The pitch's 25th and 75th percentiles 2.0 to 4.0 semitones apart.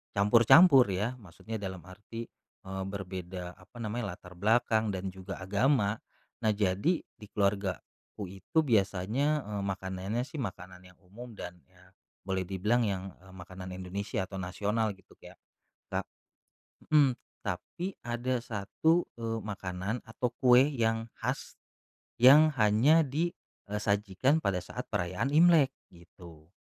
No: average, 4.6 semitones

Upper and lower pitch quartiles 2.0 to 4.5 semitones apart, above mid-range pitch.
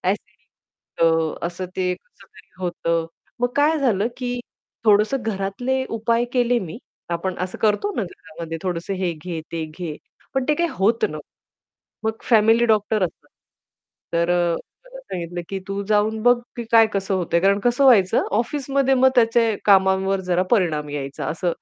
No: average, 5.1 semitones; high, 200 Hz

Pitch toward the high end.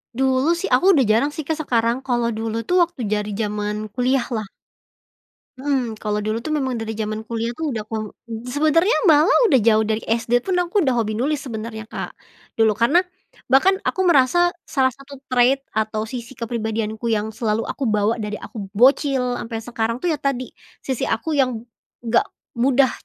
Yes: high, 235 Hz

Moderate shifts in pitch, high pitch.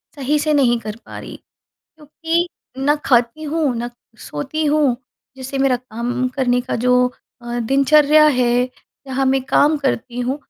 Yes: average, 3.2 semitones; very high, 265 Hz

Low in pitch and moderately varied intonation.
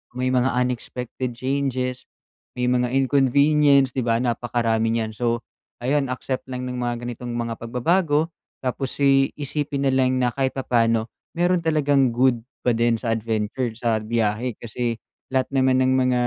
No: low, 125 Hz; narrow, 2.3 semitones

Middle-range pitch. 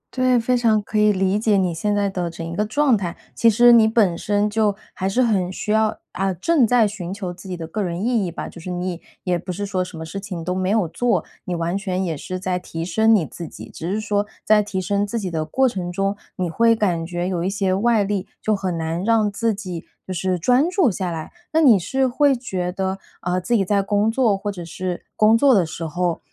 No: high, 195 Hz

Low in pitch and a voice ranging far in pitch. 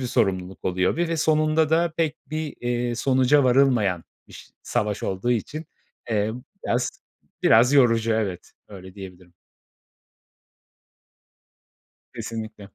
Yes: low, 120 Hz; wide, 6.1 semitones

